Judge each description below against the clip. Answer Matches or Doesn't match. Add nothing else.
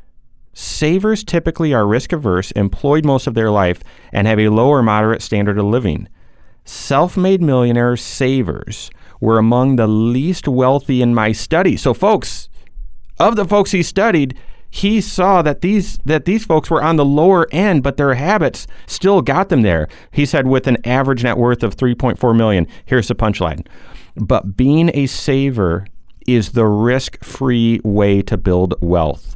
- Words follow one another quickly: Doesn't match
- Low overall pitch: Matches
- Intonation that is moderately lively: Doesn't match